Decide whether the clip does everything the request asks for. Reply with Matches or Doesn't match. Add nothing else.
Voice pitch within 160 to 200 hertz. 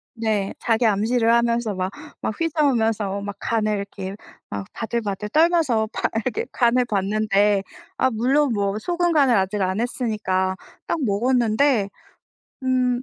Doesn't match